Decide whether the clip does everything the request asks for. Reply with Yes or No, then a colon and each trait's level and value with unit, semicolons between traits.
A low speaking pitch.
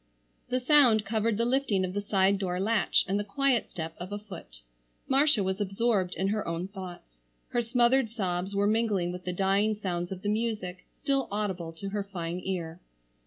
No: high, 200 Hz